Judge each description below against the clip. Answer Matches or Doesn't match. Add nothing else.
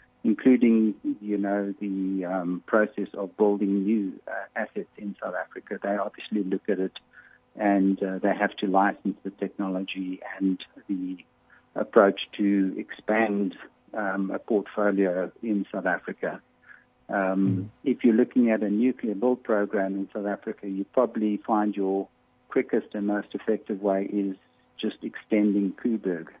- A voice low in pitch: Matches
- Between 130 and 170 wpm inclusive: Matches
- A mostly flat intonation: Matches